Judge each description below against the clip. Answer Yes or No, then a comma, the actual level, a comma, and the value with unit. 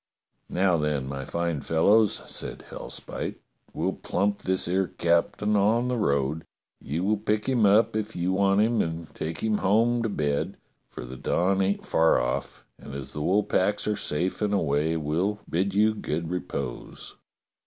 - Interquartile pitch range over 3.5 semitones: Yes, average, 4.8 semitones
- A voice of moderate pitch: No, very low, 95 Hz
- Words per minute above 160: Yes, average, 170 wpm